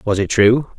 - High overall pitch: No, low, 110 Hz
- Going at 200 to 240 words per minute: Yes, fast, 230 wpm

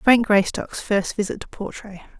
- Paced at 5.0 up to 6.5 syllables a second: No, 4.6 syllables/s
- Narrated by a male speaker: No, female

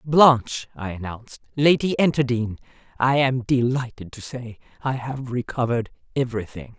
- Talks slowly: Yes, slow, 105 wpm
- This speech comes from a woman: Yes, female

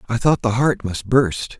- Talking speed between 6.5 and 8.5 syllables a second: No, 4.3 syllables/s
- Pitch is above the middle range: No, low, 115 Hz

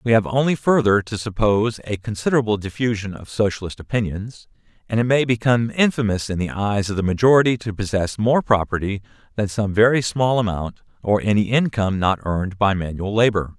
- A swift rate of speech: No, average, 175 wpm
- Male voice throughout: Yes, male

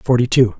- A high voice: No, low, 120 Hz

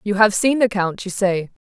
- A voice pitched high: Yes, high, 205 Hz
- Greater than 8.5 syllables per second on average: No, 4.9 syllables/s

